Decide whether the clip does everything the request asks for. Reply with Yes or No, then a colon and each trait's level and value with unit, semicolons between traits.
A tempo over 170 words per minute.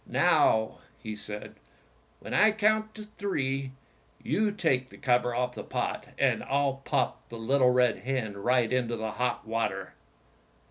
No: average, 145 wpm